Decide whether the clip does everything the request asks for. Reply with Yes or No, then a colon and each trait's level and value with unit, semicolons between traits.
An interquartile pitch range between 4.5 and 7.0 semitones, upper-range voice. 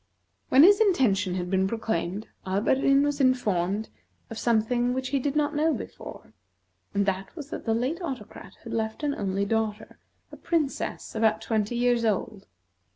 Yes: average, 5.1 semitones; high, 225 Hz